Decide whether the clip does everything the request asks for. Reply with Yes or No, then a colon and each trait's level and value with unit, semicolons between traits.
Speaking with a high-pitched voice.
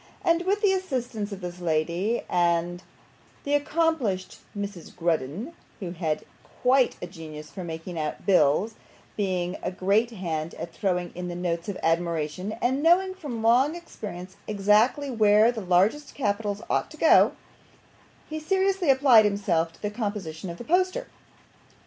Yes: high, 205 Hz